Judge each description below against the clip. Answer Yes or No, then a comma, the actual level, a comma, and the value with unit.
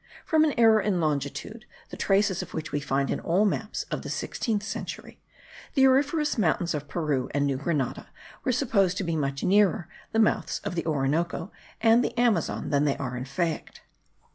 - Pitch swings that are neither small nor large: No, wide, 7.3 semitones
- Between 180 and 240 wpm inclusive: Yes, average, 190 wpm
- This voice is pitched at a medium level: Yes, medium, 175 Hz